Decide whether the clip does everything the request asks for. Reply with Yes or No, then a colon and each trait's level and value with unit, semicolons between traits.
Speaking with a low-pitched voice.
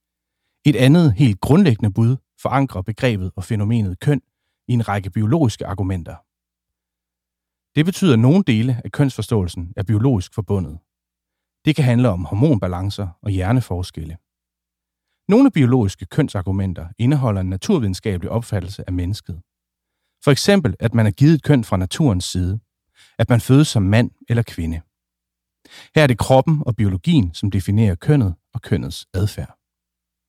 Yes: low, 100 Hz